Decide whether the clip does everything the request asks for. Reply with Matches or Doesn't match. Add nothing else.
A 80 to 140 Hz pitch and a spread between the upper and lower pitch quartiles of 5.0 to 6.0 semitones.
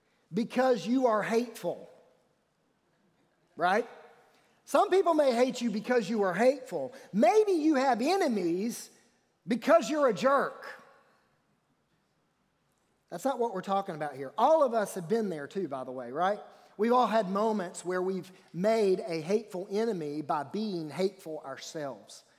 Doesn't match